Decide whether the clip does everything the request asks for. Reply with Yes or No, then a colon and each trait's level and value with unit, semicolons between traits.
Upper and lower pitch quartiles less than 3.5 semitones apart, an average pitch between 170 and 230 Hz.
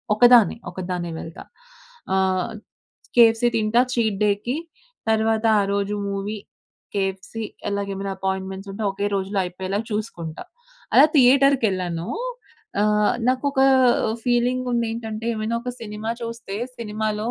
Yes: average, 3.1 semitones; high, 210 Hz